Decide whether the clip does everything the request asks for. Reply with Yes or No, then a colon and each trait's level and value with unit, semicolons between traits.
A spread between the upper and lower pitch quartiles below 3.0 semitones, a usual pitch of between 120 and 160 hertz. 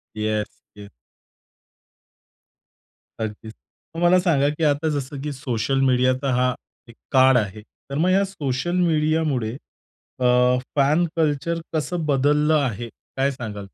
No: average, 3.8 semitones; low, 135 Hz